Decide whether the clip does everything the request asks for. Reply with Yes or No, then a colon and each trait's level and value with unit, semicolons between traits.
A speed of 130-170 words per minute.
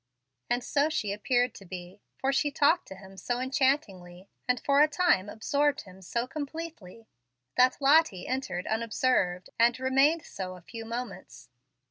Yes: average, 155 wpm